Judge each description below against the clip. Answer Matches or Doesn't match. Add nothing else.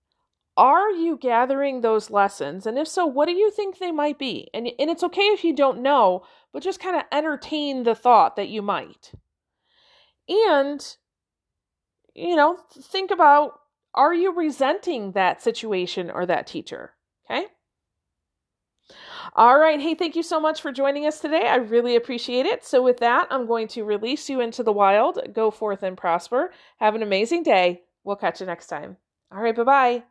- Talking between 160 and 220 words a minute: Matches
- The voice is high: Matches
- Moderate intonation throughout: Doesn't match